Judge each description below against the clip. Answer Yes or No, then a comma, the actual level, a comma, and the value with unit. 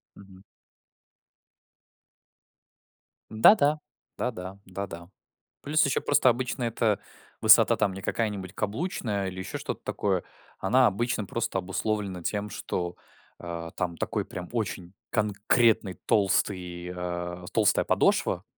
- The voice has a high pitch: No, low, 100 Hz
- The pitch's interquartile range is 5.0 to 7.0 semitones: No, average, 3.7 semitones